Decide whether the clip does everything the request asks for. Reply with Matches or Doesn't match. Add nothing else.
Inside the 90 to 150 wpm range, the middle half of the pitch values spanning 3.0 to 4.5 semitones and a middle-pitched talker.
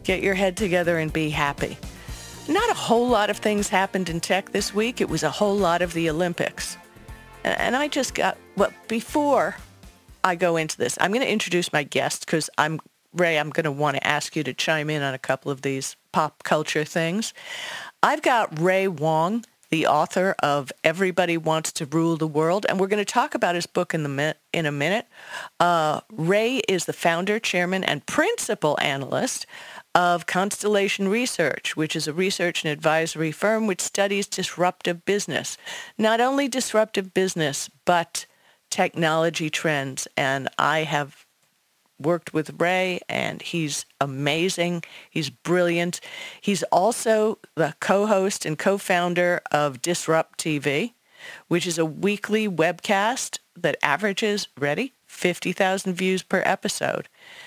Doesn't match